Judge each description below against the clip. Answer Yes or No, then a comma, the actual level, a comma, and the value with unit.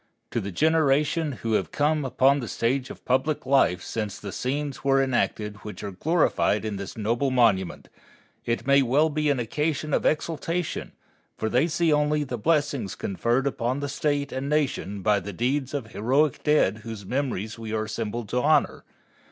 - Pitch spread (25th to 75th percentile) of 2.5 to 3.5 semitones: No, average, 5.1 semitones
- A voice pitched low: Yes, low, 130 Hz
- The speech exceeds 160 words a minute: Yes, average, 180 wpm